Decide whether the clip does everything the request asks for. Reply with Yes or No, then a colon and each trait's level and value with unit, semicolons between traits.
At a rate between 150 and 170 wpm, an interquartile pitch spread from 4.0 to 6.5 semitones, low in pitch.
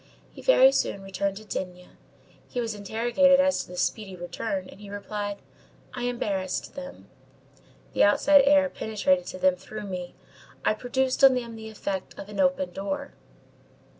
No: average, 165 wpm; average, 5.1 semitones; high, 210 Hz